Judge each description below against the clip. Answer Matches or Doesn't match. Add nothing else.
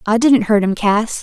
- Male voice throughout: Doesn't match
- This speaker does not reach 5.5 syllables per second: Matches